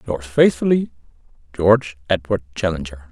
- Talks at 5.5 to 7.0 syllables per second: No, 5.3 syllables/s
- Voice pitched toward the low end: Yes, very low, 95 Hz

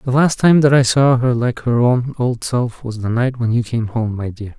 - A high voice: No, low, 120 Hz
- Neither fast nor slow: No, fast, 275 wpm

